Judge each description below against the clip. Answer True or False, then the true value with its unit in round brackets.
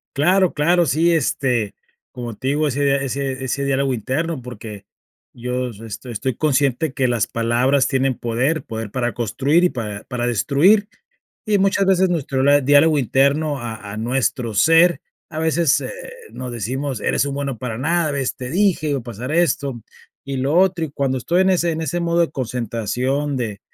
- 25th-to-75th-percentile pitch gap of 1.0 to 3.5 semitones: False (4.4 semitones)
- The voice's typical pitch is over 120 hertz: True (135 Hz)